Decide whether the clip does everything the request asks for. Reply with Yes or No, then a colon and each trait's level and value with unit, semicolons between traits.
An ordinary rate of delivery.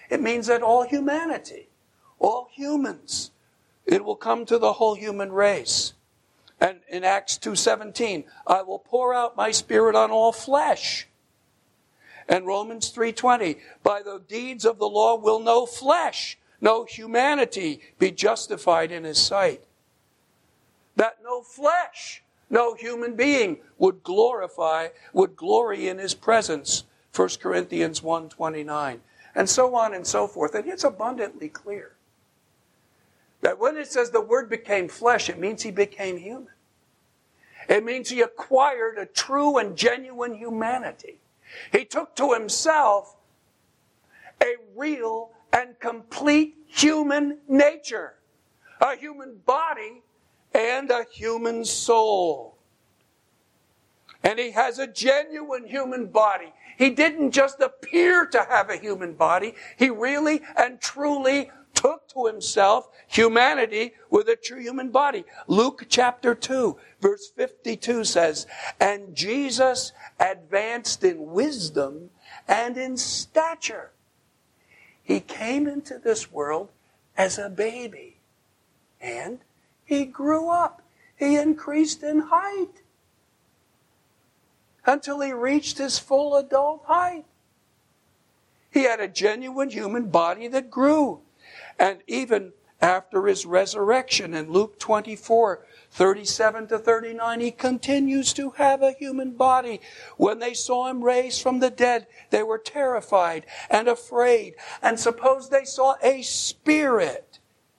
No: slow, 125 wpm